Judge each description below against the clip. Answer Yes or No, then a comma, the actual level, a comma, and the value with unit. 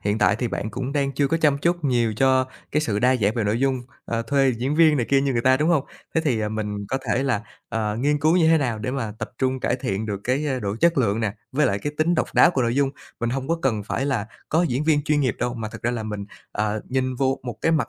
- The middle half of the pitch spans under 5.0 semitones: Yes, average, 4.4 semitones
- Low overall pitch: Yes, low, 130 Hz